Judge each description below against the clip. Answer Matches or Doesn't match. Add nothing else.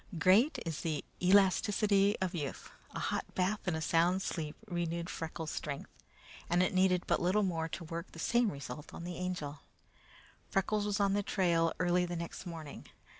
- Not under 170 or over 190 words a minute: Matches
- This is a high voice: Doesn't match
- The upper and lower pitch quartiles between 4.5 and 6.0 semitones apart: Doesn't match